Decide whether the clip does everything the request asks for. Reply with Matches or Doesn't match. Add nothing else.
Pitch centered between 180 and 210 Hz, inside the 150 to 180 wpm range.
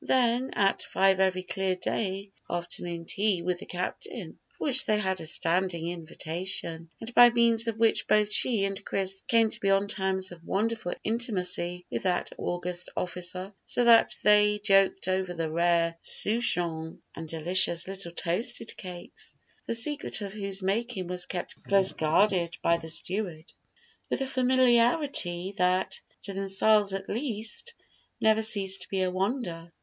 Matches